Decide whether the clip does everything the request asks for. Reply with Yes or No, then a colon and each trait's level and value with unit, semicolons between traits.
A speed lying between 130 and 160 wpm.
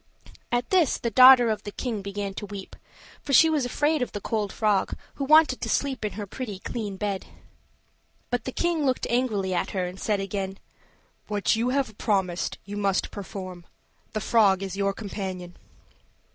No: average, 180 wpm